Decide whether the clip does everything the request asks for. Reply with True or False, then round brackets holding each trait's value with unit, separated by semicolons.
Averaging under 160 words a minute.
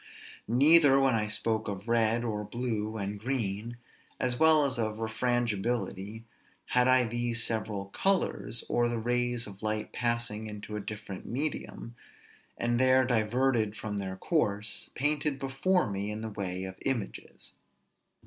True (140 wpm)